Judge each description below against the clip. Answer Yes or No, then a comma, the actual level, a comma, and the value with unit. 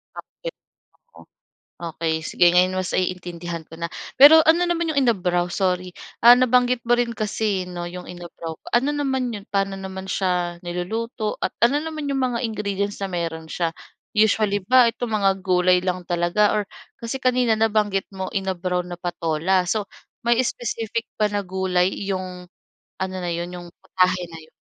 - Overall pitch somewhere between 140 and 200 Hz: Yes, high, 190 Hz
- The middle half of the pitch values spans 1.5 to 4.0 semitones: No, average, 4.5 semitones